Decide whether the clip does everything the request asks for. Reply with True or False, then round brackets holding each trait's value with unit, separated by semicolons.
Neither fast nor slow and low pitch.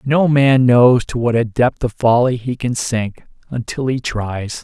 True (195 wpm; 120 Hz)